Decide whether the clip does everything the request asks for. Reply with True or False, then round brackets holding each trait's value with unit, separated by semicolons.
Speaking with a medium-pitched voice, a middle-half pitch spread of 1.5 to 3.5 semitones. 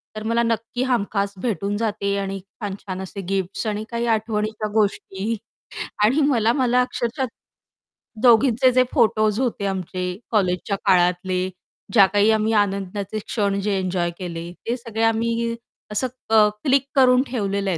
False (215 Hz; 3.0 semitones)